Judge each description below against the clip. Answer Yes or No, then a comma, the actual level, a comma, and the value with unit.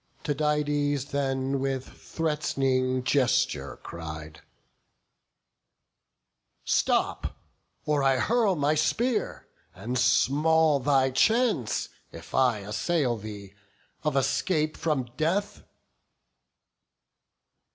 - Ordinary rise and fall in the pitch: Yes, average, 3.2 semitones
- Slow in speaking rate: Yes, slow, 80 wpm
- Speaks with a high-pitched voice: No, medium, 140 Hz